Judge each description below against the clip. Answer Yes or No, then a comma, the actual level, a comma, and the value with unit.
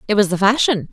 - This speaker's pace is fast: Yes, fast, 260 wpm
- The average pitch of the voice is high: Yes, high, 210 Hz